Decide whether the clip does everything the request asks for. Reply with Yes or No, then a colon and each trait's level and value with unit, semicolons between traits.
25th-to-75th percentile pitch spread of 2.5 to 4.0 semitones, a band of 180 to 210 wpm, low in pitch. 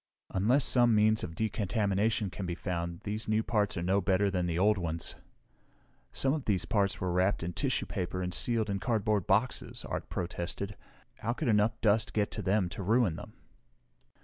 Yes: average, 3.1 semitones; average, 185 wpm; low, 100 Hz